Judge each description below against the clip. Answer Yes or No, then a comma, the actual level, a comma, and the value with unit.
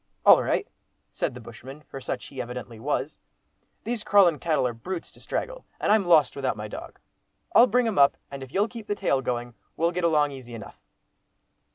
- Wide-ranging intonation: Yes, wide, 7.4 semitones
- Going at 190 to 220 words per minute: Yes, average, 200 wpm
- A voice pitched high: No, medium, 150 Hz